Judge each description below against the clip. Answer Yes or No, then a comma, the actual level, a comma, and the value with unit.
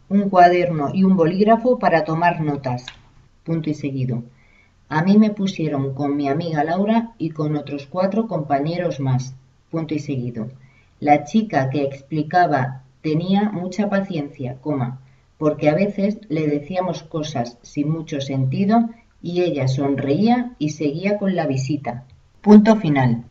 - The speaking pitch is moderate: Yes, medium, 150 Hz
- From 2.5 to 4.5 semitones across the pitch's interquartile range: No, average, 5.0 semitones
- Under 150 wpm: Yes, average, 140 wpm